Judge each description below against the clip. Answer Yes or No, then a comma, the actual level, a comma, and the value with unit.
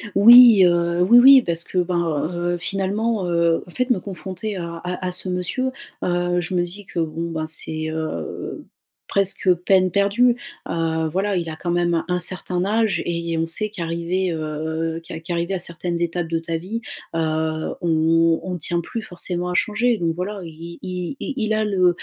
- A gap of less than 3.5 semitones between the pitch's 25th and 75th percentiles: Yes, average, 2.8 semitones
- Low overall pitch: No, medium, 175 Hz